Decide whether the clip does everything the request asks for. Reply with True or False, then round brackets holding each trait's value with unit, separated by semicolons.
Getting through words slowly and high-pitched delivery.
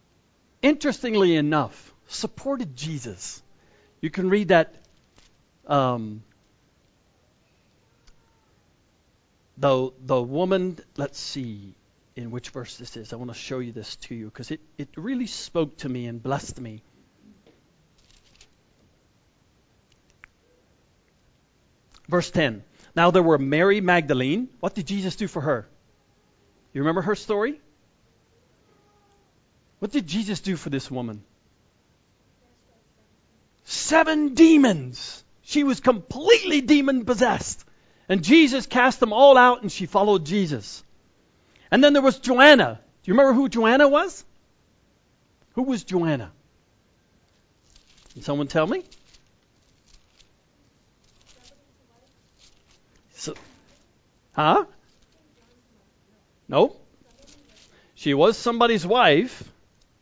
False (100 wpm; 175 Hz)